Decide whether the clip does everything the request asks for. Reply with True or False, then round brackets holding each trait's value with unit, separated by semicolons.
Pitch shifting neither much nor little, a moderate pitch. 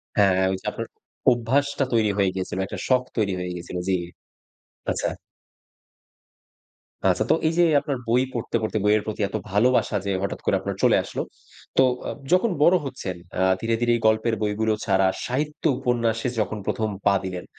False (4.2 semitones; 110 Hz)